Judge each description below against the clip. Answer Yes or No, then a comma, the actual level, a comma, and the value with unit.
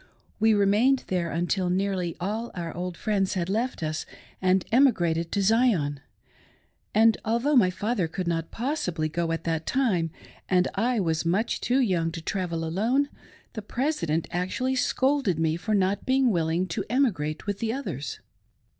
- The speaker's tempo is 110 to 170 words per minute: Yes, average, 160 wpm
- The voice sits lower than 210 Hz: Yes, high, 190 Hz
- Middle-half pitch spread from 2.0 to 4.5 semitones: No, wide, 5.5 semitones